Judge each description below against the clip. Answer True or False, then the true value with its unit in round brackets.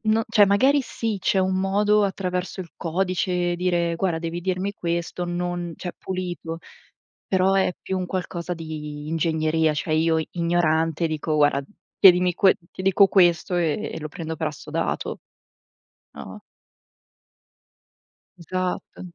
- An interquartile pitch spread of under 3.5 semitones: True (2.5 semitones)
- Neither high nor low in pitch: True (175 Hz)